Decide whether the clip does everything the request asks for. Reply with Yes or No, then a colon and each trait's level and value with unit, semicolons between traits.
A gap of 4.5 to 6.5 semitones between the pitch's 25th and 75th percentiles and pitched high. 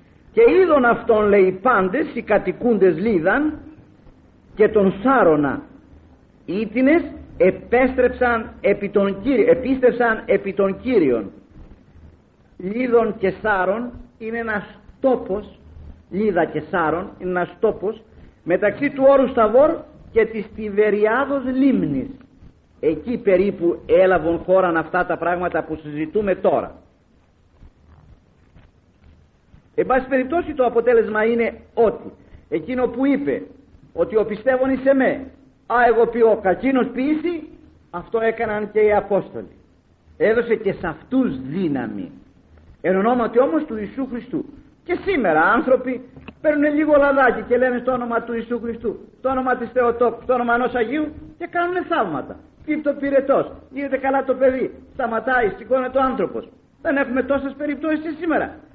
Yes: average, 5.3 semitones; high, 235 Hz